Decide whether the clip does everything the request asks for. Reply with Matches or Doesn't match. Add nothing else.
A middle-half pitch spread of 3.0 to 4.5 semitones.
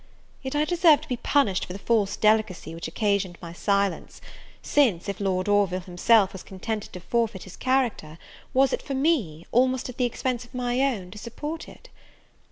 Doesn't match